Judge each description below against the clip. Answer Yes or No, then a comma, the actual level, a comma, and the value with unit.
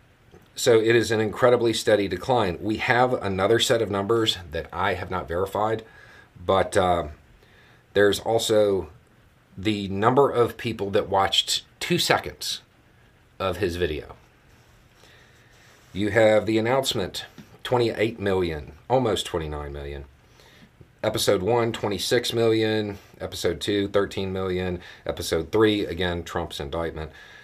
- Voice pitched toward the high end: No, low, 105 Hz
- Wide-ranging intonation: No, average, 4.4 semitones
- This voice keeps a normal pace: No, slow, 120 wpm